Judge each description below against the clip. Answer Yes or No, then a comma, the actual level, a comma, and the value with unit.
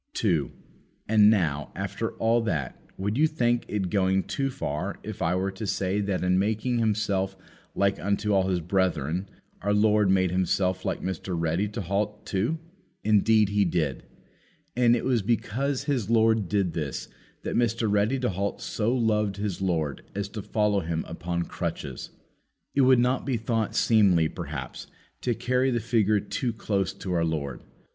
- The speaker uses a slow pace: No, average, 170 wpm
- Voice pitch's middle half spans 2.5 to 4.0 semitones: Yes, average, 3.5 semitones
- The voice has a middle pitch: No, low, 100 Hz